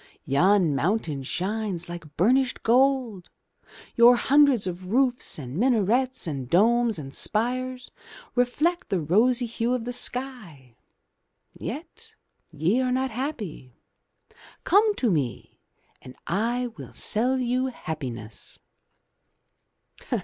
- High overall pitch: Yes, high, 225 Hz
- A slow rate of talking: Yes, slow, 110 wpm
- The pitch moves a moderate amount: No, wide, 6.8 semitones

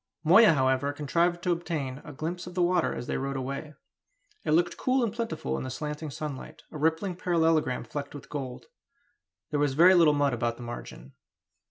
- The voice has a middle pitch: Yes, medium, 150 Hz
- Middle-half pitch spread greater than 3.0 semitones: Yes, average, 4.3 semitones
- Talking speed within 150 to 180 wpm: No, average, 190 wpm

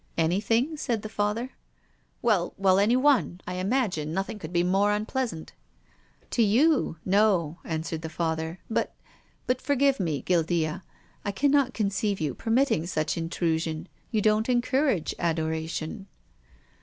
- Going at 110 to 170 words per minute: Yes, average, 155 wpm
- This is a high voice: Yes, high, 195 Hz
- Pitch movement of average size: No, wide, 6.0 semitones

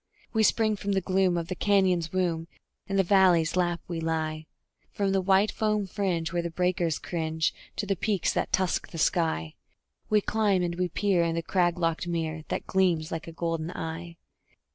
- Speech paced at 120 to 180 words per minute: No, average, 190 wpm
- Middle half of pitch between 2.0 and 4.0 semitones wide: Yes, average, 2.8 semitones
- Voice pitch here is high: No, medium, 175 Hz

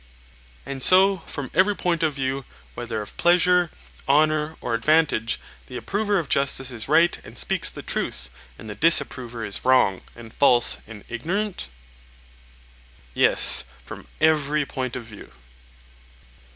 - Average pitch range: No, wide, 5.8 semitones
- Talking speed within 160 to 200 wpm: No, average, 140 wpm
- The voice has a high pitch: No, medium, 140 Hz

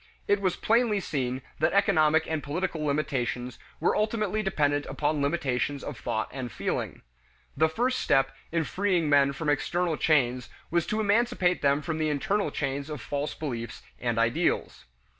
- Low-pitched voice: No, medium, 150 Hz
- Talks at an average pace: Yes, average, 160 wpm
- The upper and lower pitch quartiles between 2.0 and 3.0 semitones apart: No, average, 4.7 semitones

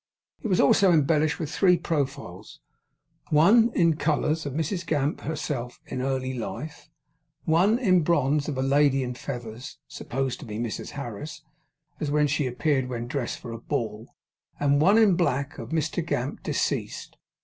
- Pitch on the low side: No, medium, 145 Hz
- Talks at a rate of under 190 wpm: Yes, average, 160 wpm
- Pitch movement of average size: Yes, average, 4.0 semitones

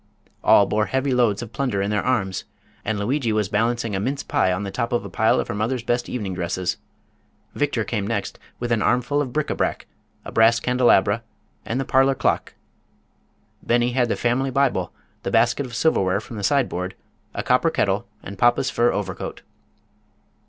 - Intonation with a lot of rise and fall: No, average, 3.6 semitones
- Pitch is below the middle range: Yes, low, 115 Hz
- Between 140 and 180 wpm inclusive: No, average, 190 wpm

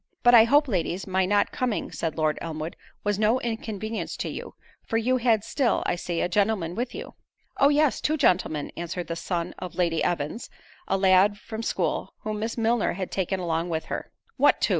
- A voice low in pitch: No, high, 200 Hz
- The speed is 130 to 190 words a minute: No, average, 200 wpm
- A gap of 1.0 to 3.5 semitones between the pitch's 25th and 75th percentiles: No, average, 4.8 semitones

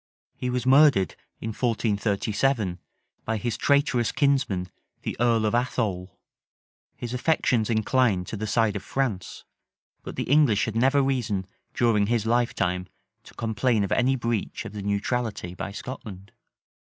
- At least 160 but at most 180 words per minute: No, average, 140 wpm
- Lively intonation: No, average, 3.7 semitones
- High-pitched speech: No, low, 115 Hz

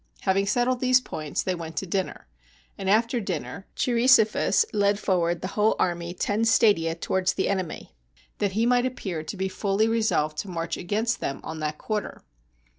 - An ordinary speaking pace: Yes, average, 180 wpm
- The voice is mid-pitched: No, high, 195 Hz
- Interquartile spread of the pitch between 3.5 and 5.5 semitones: Yes, average, 4.5 semitones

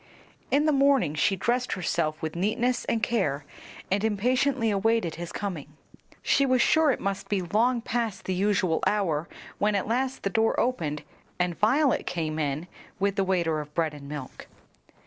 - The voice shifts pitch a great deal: Yes, wide, 6.5 semitones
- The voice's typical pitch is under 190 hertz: No, high, 200 Hz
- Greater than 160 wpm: Yes, average, 170 wpm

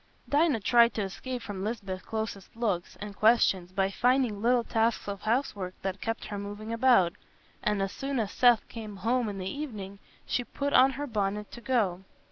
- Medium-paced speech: Yes, average, 185 wpm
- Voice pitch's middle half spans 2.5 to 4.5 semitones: Yes, average, 3.6 semitones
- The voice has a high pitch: Yes, high, 215 Hz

